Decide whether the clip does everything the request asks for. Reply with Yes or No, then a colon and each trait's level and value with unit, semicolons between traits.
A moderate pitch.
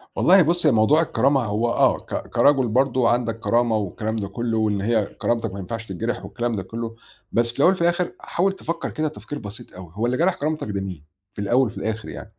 No: low, 115 Hz